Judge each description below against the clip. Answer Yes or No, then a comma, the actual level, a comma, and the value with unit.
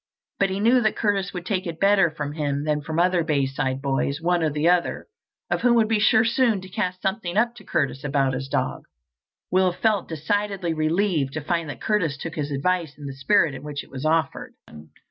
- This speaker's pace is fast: Yes, fast, 220 wpm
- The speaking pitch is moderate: Yes, medium, 165 Hz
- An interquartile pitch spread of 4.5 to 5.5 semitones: Yes, average, 5.2 semitones